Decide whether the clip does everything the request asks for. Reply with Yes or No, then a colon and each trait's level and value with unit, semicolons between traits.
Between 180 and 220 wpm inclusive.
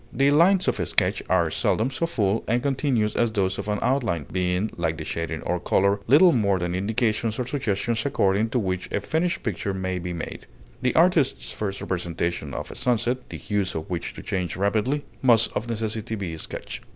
Yes: average, 200 wpm